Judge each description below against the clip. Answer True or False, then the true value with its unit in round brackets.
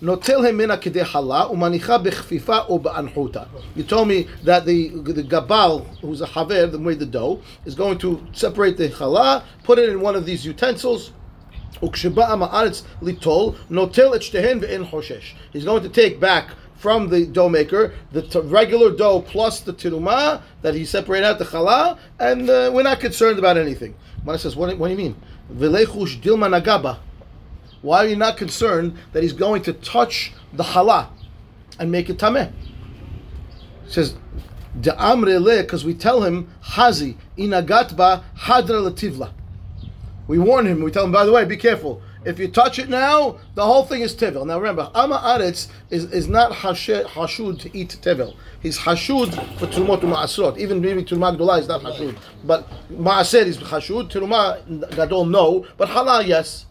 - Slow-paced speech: False (150 wpm)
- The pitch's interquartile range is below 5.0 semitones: False (5.4 semitones)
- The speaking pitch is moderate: True (180 Hz)